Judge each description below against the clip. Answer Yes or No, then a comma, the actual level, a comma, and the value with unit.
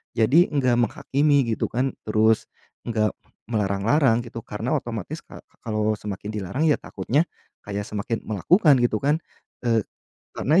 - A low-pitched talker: Yes, low, 115 Hz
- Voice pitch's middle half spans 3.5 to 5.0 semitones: Yes, average, 4.2 semitones